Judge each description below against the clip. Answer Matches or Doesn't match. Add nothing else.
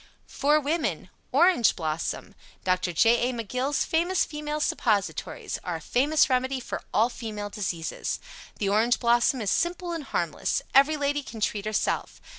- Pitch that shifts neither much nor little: Doesn't match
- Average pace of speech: Matches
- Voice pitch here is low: Doesn't match